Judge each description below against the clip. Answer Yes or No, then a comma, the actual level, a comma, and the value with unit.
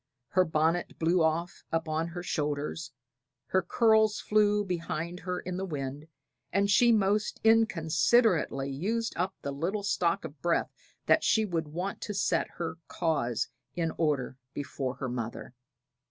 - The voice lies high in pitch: No, medium, 170 Hz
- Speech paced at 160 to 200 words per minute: No, average, 145 wpm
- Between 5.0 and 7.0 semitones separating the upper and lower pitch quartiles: No, average, 4.5 semitones